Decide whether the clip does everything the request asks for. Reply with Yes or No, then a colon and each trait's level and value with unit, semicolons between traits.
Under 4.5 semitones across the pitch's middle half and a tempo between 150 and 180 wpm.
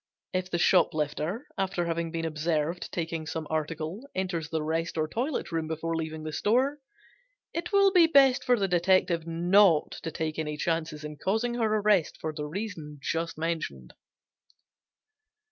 Yes: average, 4.0 semitones; average, 160 wpm